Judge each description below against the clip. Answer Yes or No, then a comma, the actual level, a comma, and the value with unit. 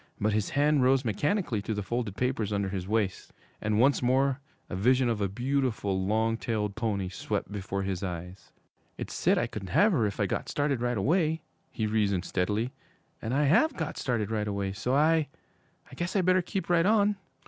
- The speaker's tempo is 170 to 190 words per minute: No, average, 200 wpm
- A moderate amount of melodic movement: No, wide, 5.9 semitones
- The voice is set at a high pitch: No, low, 115 Hz